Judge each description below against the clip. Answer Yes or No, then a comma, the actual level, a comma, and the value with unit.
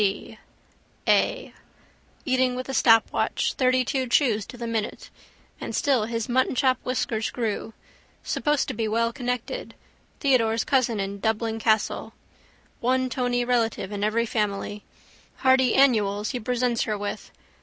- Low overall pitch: No, high, 235 Hz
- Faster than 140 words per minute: No, slow, 135 wpm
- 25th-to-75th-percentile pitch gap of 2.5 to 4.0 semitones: Yes, average, 2.8 semitones